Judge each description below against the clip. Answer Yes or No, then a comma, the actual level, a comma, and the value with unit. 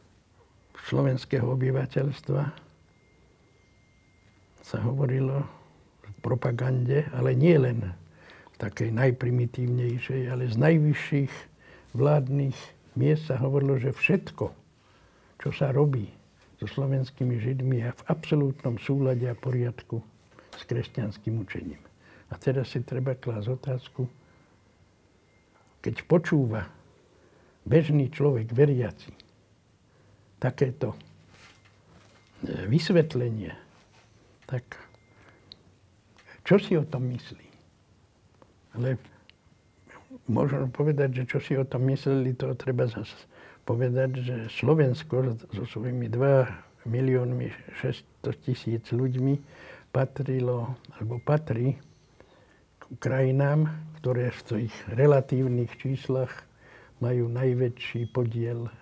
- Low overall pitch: Yes, low, 125 Hz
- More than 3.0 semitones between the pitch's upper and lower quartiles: Yes, average, 3.4 semitones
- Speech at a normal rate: No, slow, 90 wpm